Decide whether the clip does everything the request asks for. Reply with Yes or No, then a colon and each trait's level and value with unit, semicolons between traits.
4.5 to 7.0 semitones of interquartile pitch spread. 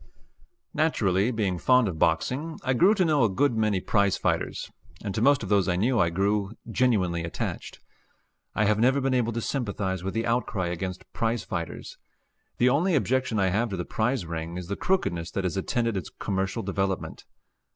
Yes: average, 5.0 semitones